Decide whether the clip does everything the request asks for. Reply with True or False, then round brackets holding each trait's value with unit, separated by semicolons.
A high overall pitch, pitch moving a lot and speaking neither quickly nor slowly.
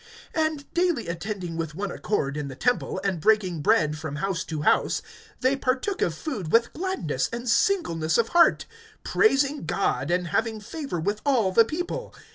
True (210 Hz; 8.7 semitones; 170 wpm)